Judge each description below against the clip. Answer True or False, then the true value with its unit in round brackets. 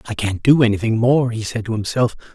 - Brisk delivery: True (230 wpm)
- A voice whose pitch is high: False (115 Hz)